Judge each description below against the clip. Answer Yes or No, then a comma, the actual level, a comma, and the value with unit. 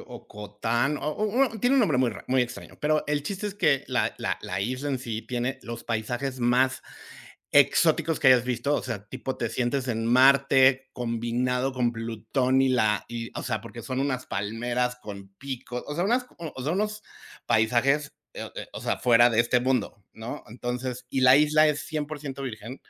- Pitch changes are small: No, average, 3.2 semitones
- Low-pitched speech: Yes, low, 130 Hz